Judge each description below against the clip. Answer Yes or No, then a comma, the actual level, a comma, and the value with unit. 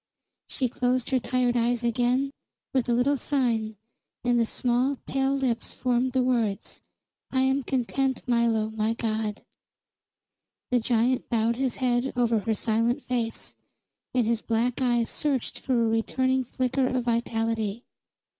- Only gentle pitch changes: Yes, narrow, 2.1 semitones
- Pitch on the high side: Yes, high, 245 Hz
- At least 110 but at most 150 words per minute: Yes, average, 145 wpm